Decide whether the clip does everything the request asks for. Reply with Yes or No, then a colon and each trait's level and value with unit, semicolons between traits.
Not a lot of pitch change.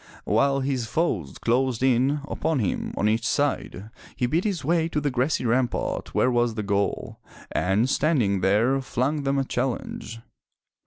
No: average, 3.8 semitones